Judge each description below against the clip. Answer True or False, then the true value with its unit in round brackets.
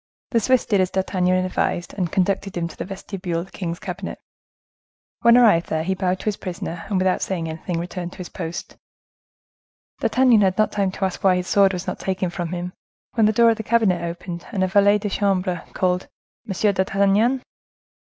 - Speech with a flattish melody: True (2.3 semitones)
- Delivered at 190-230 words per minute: True (205 wpm)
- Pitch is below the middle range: False (190 Hz)